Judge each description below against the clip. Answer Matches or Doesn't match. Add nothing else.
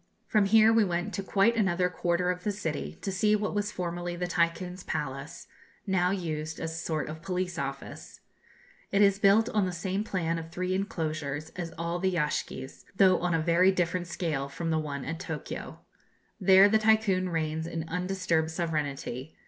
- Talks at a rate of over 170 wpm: Matches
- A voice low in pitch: Doesn't match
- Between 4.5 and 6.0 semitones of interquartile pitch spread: Doesn't match